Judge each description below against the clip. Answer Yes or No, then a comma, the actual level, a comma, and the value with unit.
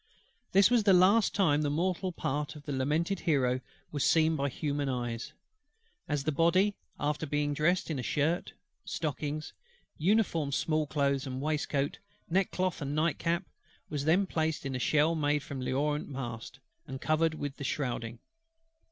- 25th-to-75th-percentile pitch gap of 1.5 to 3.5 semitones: Yes, average, 3.0 semitones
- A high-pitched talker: No, medium, 150 Hz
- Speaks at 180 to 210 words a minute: No, average, 160 wpm